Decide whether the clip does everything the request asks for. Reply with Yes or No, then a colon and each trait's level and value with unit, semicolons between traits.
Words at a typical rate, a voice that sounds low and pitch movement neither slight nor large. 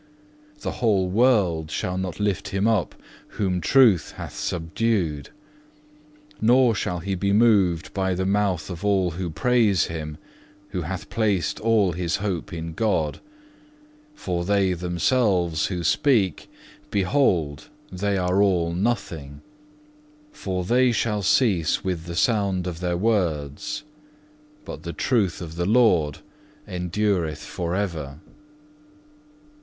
No: slow, 125 wpm; very low, 95 Hz; average, 3.5 semitones